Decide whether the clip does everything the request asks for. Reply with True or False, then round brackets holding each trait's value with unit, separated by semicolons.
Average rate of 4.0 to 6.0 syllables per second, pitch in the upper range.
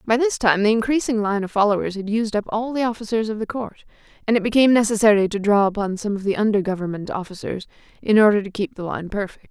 False (6.5 syllables/s; 210 Hz)